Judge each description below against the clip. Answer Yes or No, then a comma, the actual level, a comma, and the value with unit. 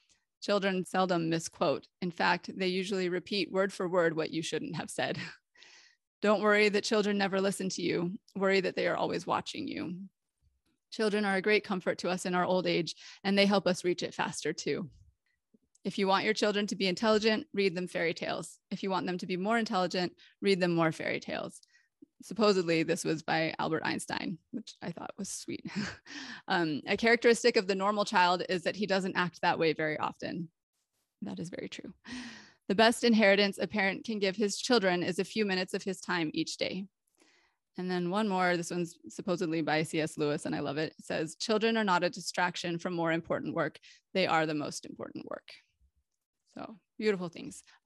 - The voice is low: No, high, 190 Hz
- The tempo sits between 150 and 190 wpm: No, average, 200 wpm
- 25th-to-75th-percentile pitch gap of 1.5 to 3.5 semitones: Yes, average, 3.1 semitones